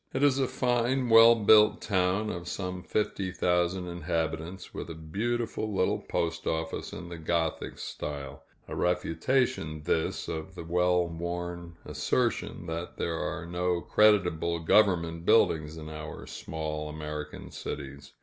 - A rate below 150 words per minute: Yes, slow, 135 wpm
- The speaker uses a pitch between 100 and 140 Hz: No, very low, 85 Hz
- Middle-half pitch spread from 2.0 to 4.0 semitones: Yes, average, 3.4 semitones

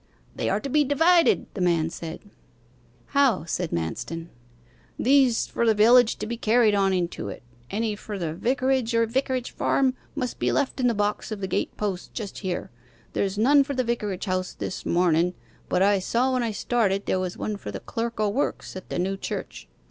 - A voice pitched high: Yes, high, 215 Hz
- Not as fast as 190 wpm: No, average, 200 wpm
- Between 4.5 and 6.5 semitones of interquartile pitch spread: Yes, average, 5.2 semitones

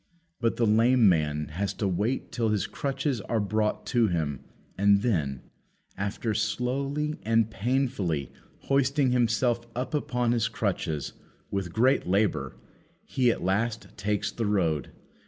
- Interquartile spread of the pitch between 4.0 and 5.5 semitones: Yes, average, 4.4 semitones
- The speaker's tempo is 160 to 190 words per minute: No, slow, 135 wpm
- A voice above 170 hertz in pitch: No, low, 110 Hz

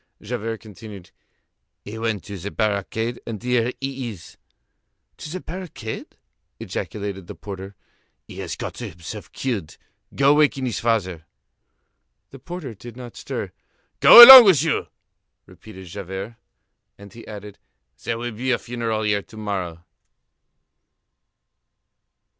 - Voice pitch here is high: No, low, 110 Hz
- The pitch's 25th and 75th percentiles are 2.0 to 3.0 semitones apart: No, average, 3.7 semitones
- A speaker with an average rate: No, slow, 130 wpm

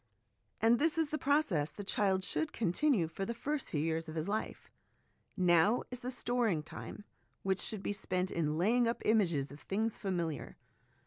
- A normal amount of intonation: No, wide, 6.2 semitones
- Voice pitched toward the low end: No, high, 200 Hz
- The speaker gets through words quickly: No, average, 180 wpm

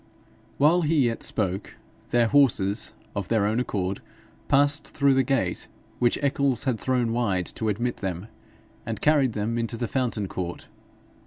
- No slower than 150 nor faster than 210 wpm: Yes, average, 155 wpm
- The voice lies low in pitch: Yes, low, 120 Hz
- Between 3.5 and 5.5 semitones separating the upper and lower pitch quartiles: Yes, average, 4.6 semitones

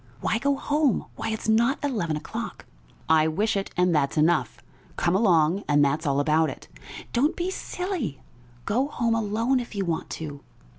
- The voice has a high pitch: Yes, high, 195 Hz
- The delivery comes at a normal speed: Yes, average, 170 wpm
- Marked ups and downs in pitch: Yes, wide, 7.4 semitones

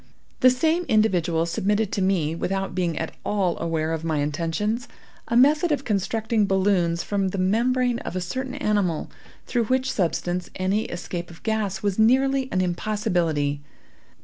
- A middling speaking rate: Yes, average, 155 wpm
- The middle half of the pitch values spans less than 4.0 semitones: No, average, 5.0 semitones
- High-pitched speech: Yes, high, 195 Hz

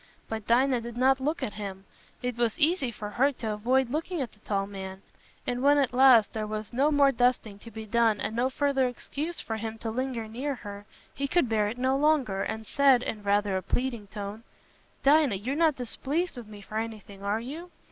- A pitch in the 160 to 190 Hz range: No, high, 235 Hz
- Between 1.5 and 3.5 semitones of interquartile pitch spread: No, average, 4.2 semitones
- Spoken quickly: Yes, fast, 210 wpm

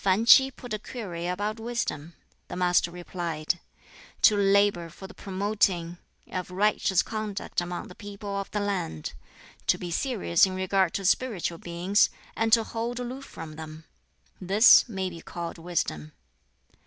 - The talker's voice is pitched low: No, high, 190 Hz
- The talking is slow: No, average, 155 wpm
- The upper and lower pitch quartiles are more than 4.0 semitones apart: No, average, 3.6 semitones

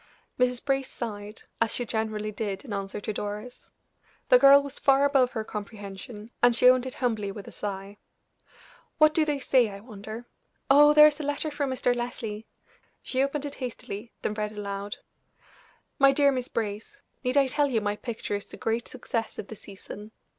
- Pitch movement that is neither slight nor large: Yes, average, 4.5 semitones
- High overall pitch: Yes, high, 235 Hz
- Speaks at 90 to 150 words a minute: No, average, 190 wpm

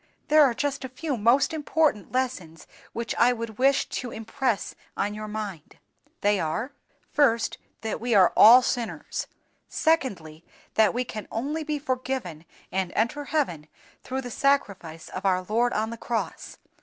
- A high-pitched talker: Yes, high, 235 Hz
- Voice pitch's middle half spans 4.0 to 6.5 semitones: Yes, average, 4.5 semitones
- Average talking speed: Yes, average, 155 wpm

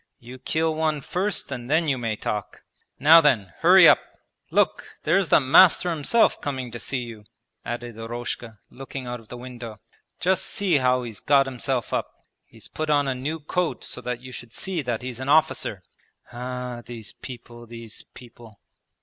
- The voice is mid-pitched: No, low, 125 Hz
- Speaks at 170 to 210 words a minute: Yes, average, 175 wpm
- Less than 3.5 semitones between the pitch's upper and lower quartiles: No, average, 4.0 semitones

